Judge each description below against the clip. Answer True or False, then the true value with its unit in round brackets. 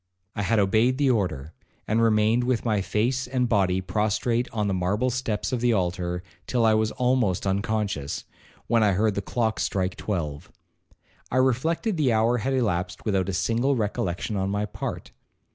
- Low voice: True (110 Hz)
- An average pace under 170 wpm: False (175 wpm)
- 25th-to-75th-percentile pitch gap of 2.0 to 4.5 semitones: True (4.1 semitones)